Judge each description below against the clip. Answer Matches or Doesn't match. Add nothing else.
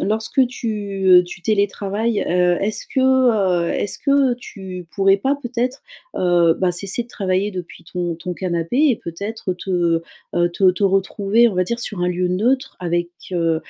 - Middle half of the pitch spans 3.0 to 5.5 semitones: Matches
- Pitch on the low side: Doesn't match